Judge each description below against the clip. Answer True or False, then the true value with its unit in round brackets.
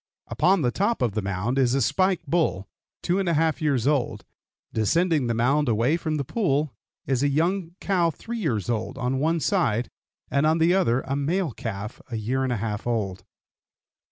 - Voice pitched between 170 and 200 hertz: False (140 Hz)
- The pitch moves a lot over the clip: True (6.2 semitones)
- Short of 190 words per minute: False (195 wpm)